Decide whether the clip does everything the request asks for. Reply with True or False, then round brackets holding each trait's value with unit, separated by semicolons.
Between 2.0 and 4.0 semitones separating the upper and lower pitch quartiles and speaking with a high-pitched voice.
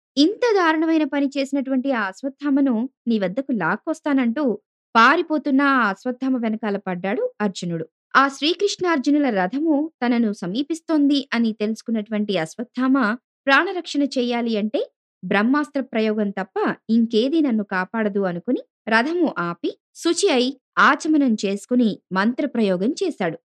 False (5.3 semitones; 255 Hz)